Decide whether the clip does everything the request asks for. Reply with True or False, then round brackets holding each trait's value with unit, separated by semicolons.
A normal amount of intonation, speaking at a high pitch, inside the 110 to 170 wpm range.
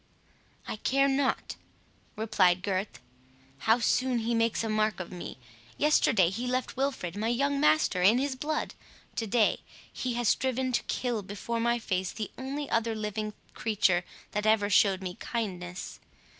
True (4.2 semitones; 225 Hz; 155 wpm)